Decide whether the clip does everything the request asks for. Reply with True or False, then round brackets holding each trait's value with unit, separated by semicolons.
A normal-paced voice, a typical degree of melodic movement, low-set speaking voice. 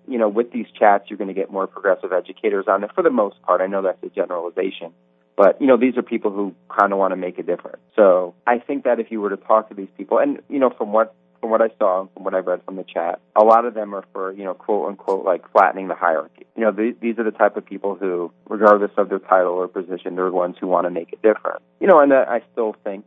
False (290 wpm; 3.0 semitones; 100 Hz)